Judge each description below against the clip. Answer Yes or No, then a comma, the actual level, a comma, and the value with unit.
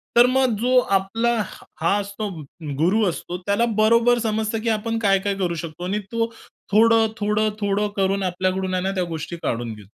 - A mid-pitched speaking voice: No, high, 205 Hz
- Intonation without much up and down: No, average, 3.3 semitones